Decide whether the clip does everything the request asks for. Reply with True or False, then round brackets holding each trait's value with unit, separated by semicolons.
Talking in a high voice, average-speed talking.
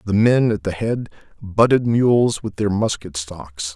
False (105 Hz; 175 wpm)